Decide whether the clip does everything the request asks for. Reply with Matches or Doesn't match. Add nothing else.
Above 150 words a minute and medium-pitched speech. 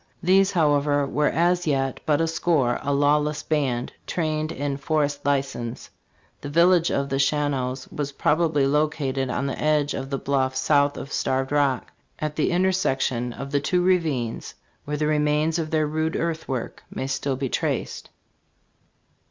Matches